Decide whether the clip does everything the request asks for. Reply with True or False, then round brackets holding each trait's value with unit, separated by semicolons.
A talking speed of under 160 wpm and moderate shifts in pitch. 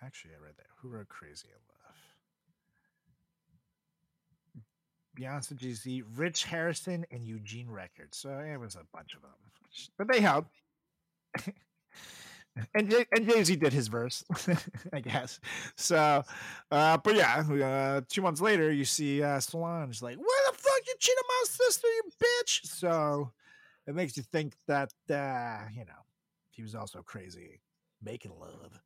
False (150 wpm; 6.1 semitones)